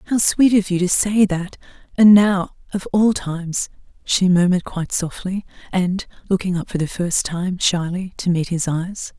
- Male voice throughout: No, female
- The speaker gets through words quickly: No, average, 185 wpm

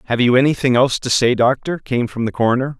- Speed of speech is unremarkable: No, fast, 235 wpm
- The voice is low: Yes, low, 125 Hz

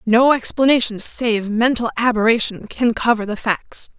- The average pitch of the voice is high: Yes, high, 230 Hz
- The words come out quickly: No, slow, 135 wpm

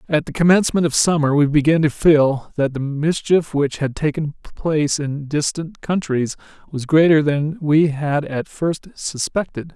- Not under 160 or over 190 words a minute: Yes, average, 165 wpm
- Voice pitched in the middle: Yes, medium, 150 Hz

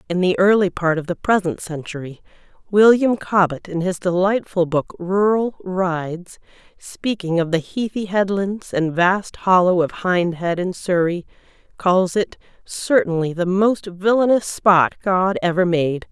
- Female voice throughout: Yes, female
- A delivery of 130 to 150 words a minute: Yes, average, 140 wpm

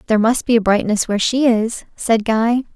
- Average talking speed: Yes, average, 195 wpm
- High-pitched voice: Yes, high, 225 Hz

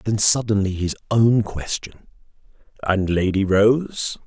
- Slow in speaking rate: Yes, slow, 100 wpm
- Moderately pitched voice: No, low, 110 Hz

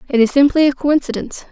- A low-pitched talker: No, very high, 275 Hz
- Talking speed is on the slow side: No, average, 200 wpm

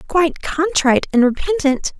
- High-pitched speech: Yes, very high, 305 Hz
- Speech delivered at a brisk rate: No, slow, 120 wpm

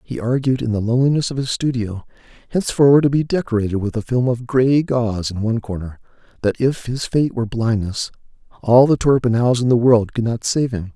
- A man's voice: Yes, male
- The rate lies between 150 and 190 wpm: No, fast, 205 wpm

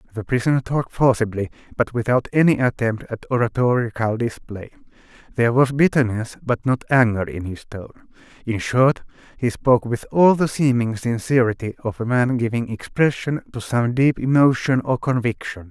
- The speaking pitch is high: No, low, 120 Hz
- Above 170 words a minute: No, average, 155 wpm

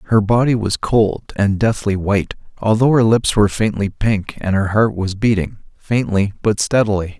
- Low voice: Yes, low, 105 Hz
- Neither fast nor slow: Yes, average, 175 wpm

